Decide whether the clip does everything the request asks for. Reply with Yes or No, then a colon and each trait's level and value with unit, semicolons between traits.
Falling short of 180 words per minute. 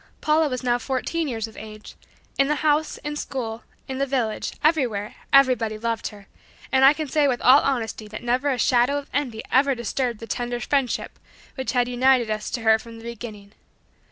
No: average, 195 wpm